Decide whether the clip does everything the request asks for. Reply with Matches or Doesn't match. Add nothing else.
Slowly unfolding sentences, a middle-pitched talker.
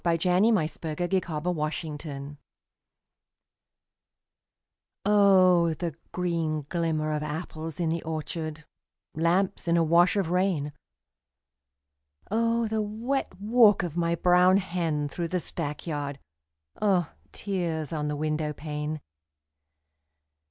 Matches